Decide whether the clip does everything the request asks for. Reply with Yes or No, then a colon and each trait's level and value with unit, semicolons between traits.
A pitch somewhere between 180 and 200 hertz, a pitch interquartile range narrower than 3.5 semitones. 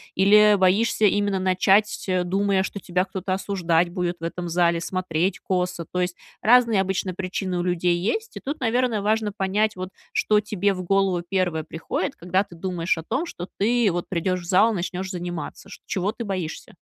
Yes: medium, 185 Hz; narrow, 2.5 semitones